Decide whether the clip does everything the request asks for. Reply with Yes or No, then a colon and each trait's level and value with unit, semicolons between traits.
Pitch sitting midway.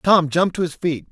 Yes: medium, 165 Hz